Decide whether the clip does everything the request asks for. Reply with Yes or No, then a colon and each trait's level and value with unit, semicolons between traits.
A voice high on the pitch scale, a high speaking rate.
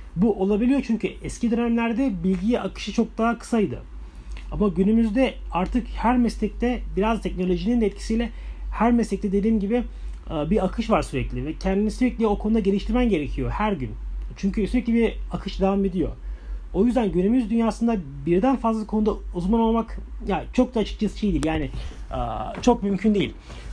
Yes: high, 210 Hz; fast, 155 wpm